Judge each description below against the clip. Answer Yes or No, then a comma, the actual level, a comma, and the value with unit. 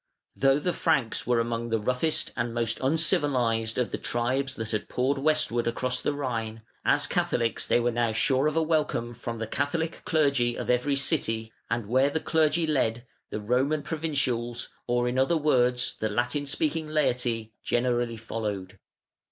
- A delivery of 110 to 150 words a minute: No, average, 170 wpm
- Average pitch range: Yes, average, 3.6 semitones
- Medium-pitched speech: No, low, 125 Hz